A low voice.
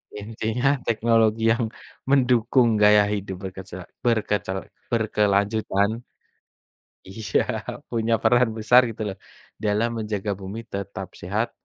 Yes: low, 110 Hz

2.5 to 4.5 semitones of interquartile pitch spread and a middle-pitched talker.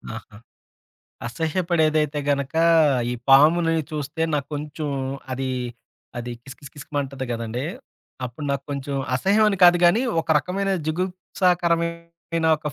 Yes: average, 3.5 semitones; medium, 155 Hz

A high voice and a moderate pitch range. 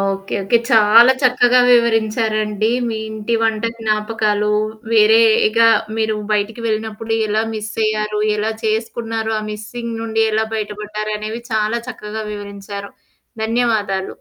No: high, 220 Hz; narrow, 1.1 semitones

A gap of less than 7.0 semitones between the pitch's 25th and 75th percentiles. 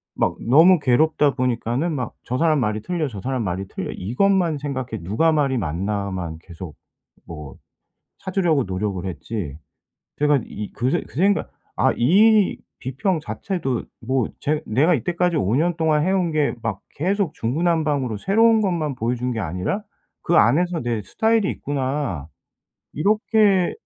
No: wide, 7.7 semitones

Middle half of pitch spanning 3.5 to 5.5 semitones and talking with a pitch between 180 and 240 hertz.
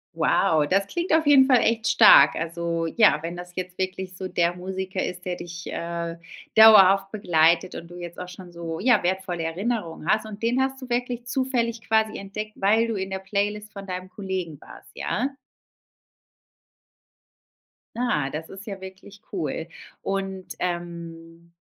Yes: average, 4.1 semitones; high, 190 Hz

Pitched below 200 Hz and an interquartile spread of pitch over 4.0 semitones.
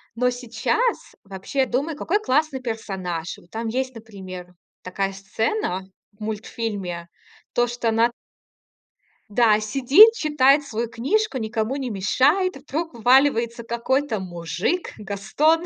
No: high, 235 Hz; average, 5.3 semitones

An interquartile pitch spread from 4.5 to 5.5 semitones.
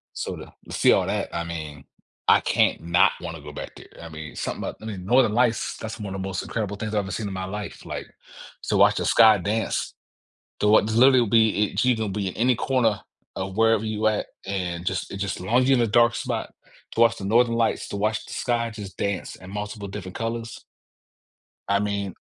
No: average, 3.0 semitones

